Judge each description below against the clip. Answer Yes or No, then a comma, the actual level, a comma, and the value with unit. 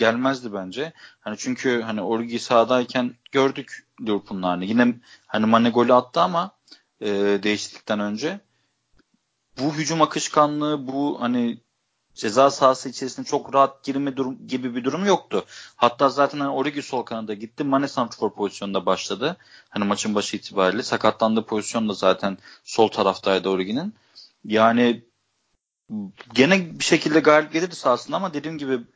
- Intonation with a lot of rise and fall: No, average, 4.1 semitones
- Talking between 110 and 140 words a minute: Yes, average, 135 wpm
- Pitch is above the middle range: No, low, 120 Hz